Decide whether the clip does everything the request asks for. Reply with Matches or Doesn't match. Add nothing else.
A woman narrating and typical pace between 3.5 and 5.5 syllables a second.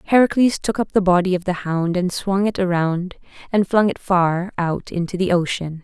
Matches